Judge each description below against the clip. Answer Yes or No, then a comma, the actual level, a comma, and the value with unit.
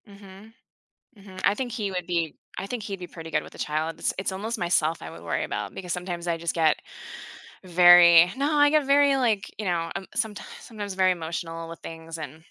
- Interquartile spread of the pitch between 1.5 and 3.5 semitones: No, average, 3.9 semitones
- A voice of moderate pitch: Yes, medium, 180 Hz